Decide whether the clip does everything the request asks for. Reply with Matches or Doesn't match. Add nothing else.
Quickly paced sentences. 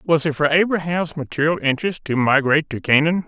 Doesn't match